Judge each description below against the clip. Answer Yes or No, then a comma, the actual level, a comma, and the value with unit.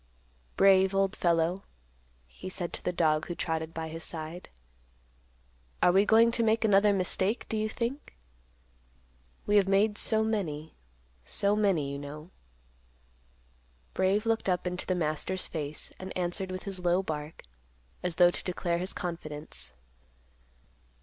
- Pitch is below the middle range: No, medium, 185 Hz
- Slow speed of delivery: No, average, 145 wpm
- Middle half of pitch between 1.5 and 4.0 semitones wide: Yes, average, 3.5 semitones